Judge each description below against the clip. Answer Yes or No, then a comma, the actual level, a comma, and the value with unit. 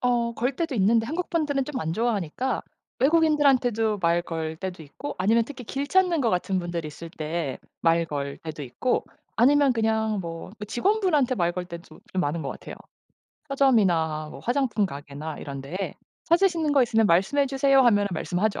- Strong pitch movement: Yes, wide, 8.2 semitones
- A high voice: Yes, high, 220 Hz